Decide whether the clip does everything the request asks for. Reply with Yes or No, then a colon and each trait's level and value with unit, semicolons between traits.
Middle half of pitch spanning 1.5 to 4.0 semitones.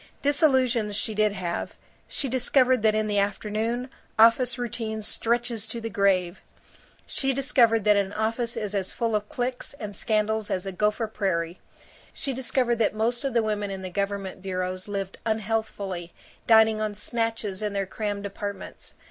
Yes: average, 2.7 semitones